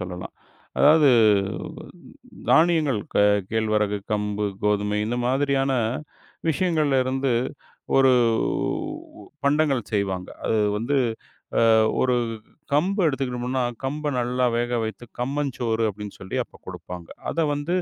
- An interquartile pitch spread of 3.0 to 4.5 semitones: No, average, 5.2 semitones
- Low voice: Yes, low, 125 Hz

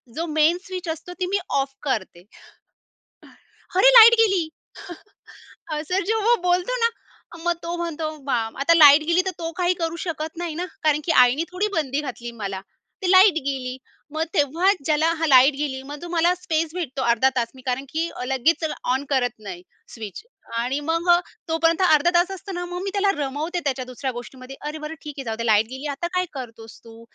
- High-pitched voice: Yes, very high, 315 Hz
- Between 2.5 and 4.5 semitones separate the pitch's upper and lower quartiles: No, average, 4.9 semitones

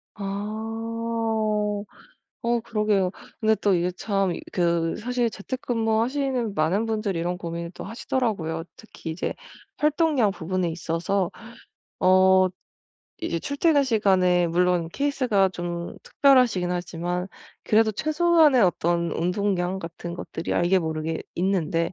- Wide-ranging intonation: No, average, 4.6 semitones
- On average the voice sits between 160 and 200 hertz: Yes, high, 190 Hz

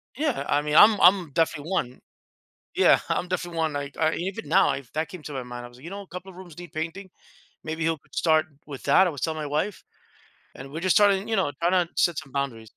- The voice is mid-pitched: Yes, medium, 165 Hz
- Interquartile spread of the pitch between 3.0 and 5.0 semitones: Yes, average, 4.4 semitones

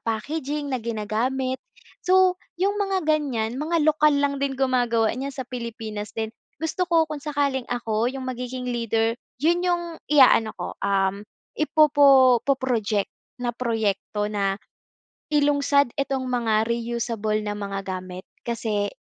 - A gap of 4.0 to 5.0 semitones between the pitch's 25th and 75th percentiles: Yes, average, 4.6 semitones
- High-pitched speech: Yes, very high, 250 Hz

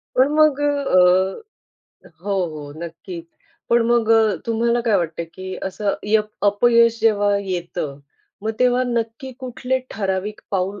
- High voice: Yes, high, 215 Hz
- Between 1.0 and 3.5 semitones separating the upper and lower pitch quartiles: No, average, 4.1 semitones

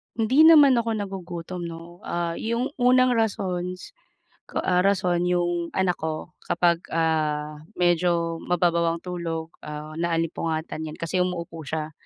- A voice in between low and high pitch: Yes, medium, 175 Hz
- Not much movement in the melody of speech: Yes, narrow, 2.0 semitones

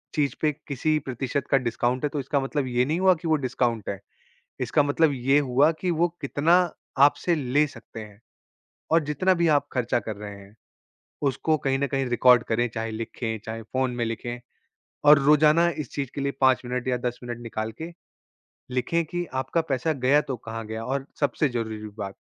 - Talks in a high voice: No, low, 130 Hz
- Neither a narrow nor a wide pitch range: Yes, average, 3.9 semitones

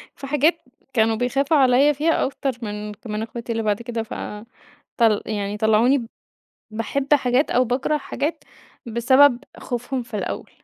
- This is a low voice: No, high, 245 Hz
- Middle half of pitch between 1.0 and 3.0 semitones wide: No, average, 3.7 semitones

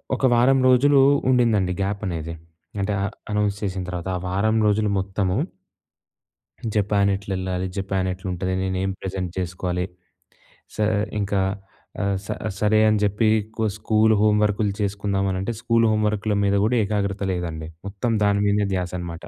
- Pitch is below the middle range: Yes, low, 100 Hz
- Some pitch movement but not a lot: No, narrow, 2.3 semitones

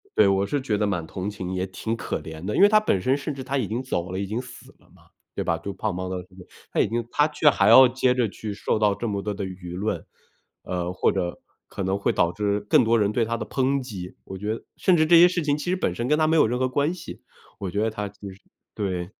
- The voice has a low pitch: Yes, low, 105 Hz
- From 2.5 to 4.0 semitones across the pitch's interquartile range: No, wide, 5.4 semitones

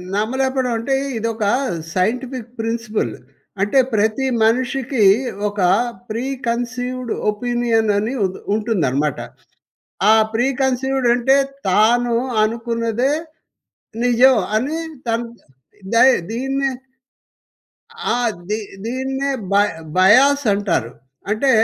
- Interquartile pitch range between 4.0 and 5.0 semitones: No, average, 3.1 semitones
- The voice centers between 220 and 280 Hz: Yes, high, 235 Hz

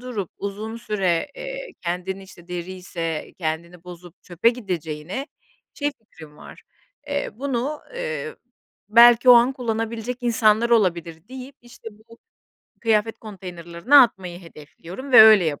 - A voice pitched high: Yes, high, 210 Hz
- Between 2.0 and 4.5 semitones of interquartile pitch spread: No, wide, 5.6 semitones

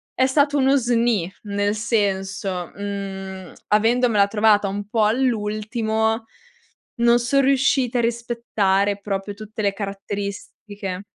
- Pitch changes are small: No, average, 3.0 semitones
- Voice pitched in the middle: No, high, 215 Hz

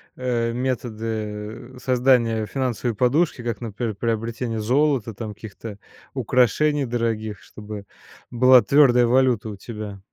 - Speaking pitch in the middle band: No, low, 115 Hz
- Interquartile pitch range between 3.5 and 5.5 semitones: No, average, 2.8 semitones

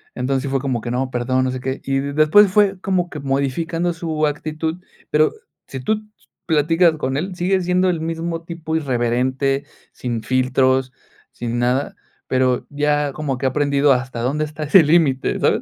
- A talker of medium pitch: Yes, medium, 145 Hz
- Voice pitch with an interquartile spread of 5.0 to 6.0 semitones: No, average, 4.1 semitones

